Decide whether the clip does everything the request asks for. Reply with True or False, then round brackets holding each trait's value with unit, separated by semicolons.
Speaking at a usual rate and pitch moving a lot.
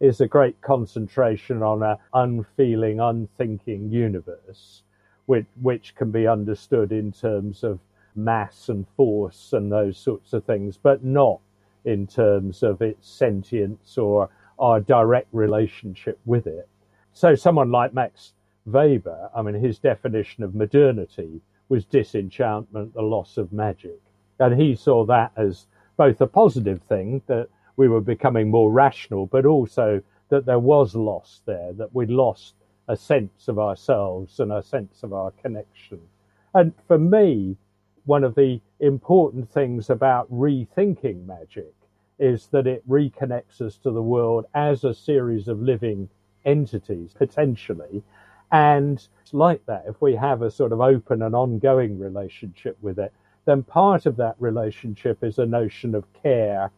False (150 wpm; 4.3 semitones)